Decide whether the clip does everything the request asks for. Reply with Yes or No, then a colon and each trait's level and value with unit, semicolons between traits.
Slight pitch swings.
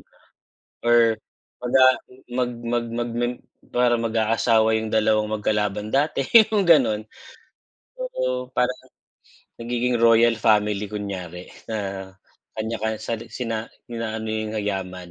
Yes: narrow, 2.3 semitones